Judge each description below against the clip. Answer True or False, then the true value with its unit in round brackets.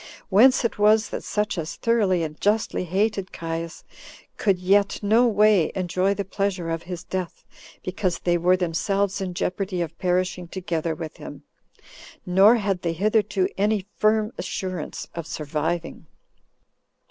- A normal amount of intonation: True (3.2 semitones)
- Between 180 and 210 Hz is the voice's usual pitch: True (185 Hz)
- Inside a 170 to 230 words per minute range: False (145 wpm)